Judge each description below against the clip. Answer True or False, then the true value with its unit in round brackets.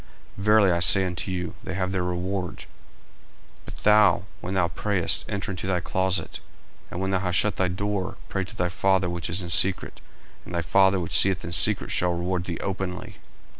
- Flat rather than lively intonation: True (1.6 semitones)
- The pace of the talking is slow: False (200 wpm)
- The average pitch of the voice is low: True (95 Hz)